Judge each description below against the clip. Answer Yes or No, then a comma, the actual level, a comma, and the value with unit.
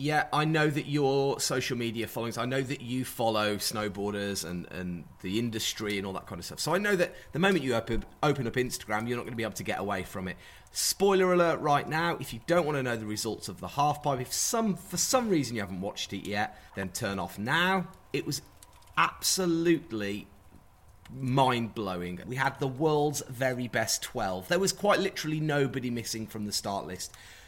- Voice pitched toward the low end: Yes, low, 125 Hz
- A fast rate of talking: Yes, fast, 210 wpm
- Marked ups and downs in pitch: Yes, wide, 6.4 semitones